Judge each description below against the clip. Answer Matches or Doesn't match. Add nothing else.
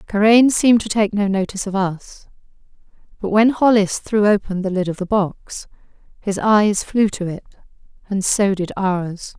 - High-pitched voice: Matches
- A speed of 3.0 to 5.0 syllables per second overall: Matches